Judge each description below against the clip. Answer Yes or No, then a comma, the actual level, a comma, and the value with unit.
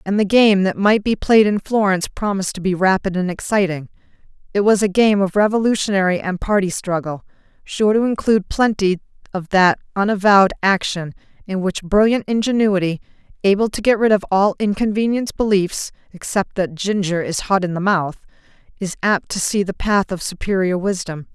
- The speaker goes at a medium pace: Yes, average, 170 wpm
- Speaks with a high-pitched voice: Yes, high, 195 Hz